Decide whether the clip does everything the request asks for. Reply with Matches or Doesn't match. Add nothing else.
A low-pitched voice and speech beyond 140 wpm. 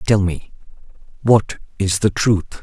Doesn't match